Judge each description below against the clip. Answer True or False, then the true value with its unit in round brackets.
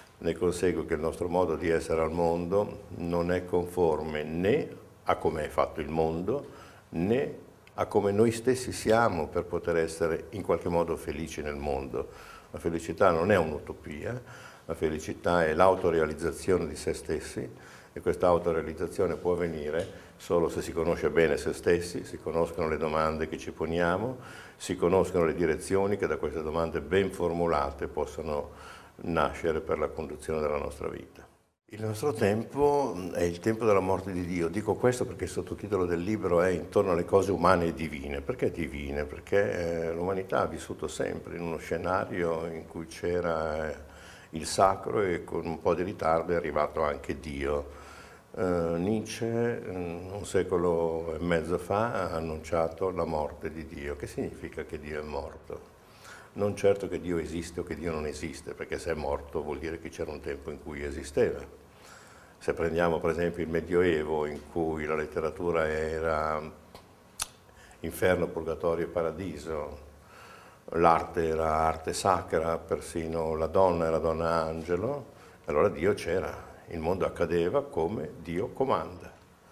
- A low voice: True (85 Hz)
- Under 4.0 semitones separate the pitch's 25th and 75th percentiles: True (2.6 semitones)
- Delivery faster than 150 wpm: True (160 wpm)